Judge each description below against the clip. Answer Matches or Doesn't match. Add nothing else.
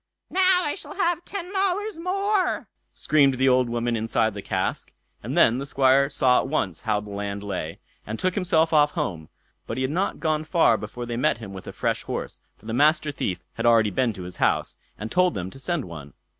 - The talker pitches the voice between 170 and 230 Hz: Doesn't match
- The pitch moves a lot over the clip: Matches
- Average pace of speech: Doesn't match